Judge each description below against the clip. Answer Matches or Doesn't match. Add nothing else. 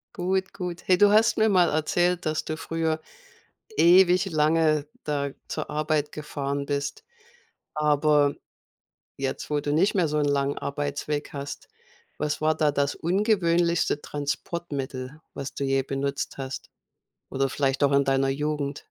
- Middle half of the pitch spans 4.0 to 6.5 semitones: Doesn't match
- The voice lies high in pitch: Doesn't match